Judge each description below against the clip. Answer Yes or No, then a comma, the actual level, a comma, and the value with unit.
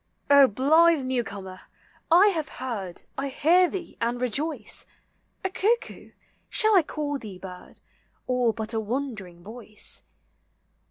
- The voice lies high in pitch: Yes, very high, 255 Hz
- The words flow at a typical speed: No, slow, 130 wpm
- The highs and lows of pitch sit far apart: Yes, wide, 6.8 semitones